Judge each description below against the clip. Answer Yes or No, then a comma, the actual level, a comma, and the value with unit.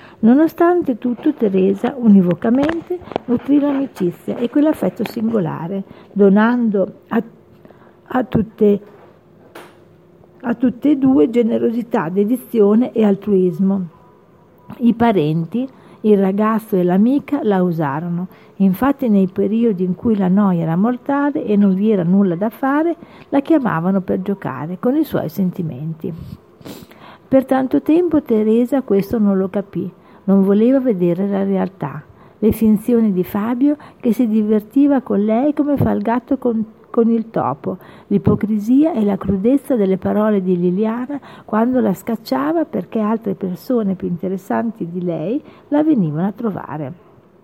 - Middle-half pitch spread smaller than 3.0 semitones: No, average, 4.3 semitones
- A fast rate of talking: No, average, 135 wpm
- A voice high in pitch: Yes, high, 215 Hz